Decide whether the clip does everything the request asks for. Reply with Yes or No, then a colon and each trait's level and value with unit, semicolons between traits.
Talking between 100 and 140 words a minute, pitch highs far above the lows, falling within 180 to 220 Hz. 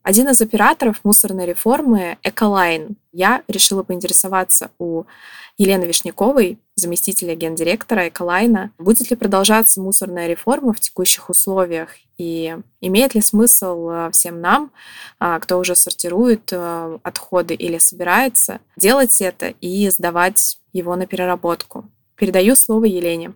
No: average, 115 wpm; average, 4.0 semitones; high, 190 Hz